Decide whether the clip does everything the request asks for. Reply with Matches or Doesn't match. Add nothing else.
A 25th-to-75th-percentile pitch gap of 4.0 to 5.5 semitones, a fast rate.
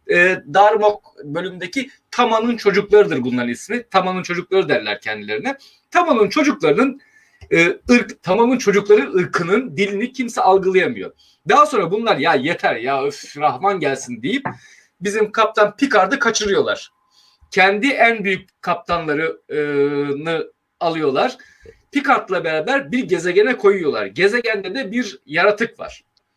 Doesn't match